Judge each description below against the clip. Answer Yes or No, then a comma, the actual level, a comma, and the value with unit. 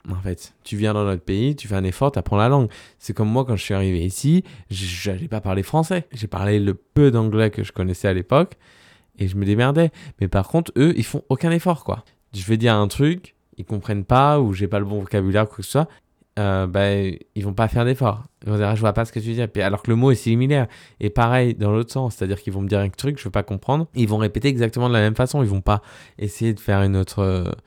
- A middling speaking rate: No, fast, 275 wpm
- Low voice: Yes, low, 110 Hz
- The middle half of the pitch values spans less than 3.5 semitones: No, average, 4.3 semitones